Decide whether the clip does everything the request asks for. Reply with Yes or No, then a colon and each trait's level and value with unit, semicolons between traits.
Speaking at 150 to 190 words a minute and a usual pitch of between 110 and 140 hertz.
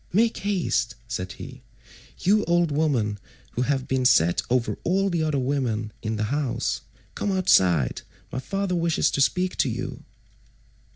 Yes: average, 155 wpm; low, 135 Hz